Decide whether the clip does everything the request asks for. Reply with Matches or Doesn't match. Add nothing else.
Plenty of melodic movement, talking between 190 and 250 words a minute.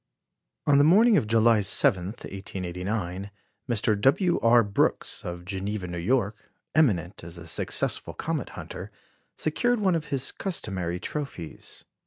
Doesn't match